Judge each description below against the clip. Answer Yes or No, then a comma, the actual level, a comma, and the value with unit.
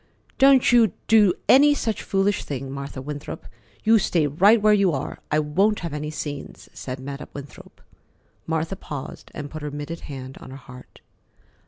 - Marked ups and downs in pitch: Yes, wide, 6.4 semitones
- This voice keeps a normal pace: Yes, average, 170 wpm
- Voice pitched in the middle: Yes, medium, 155 Hz